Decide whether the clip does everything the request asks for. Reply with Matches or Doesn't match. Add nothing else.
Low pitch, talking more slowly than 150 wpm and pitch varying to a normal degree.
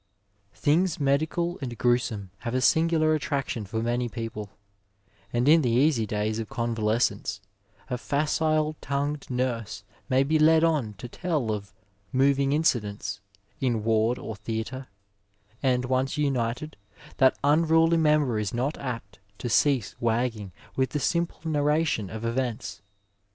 Matches